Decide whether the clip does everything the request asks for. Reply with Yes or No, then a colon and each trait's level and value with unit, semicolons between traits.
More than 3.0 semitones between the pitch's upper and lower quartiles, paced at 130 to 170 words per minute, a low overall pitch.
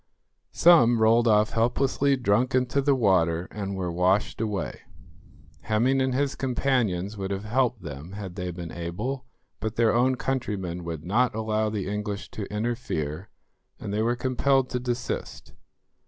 Yes: average, 4.6 semitones; average, 155 wpm; low, 110 Hz